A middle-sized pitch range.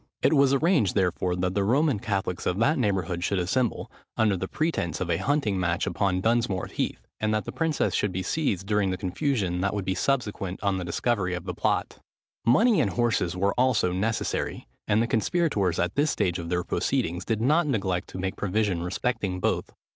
Yes: average, 4.7 semitones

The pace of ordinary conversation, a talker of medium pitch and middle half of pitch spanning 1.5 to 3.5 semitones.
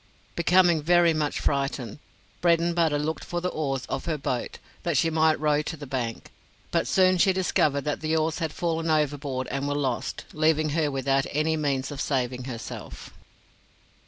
Yes: average, 170 wpm; medium, 150 Hz; average, 3.0 semitones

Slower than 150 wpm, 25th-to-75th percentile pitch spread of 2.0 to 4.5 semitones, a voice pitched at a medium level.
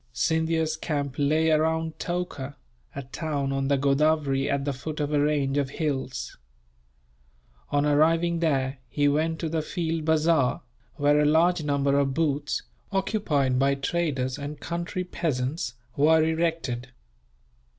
Yes: average, 140 wpm; narrow, 2.6 semitones; medium, 150 Hz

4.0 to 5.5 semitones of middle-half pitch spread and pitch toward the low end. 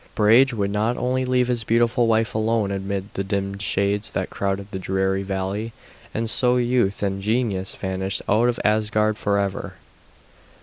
No: average, 2.8 semitones; low, 105 Hz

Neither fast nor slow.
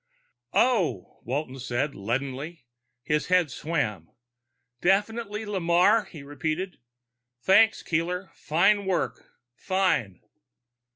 No: slow, 90 wpm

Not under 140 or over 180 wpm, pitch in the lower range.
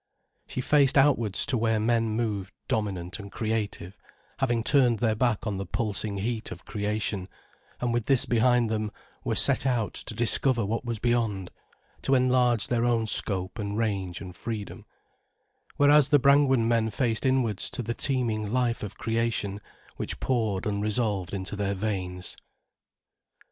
Yes: average, 155 wpm; low, 110 Hz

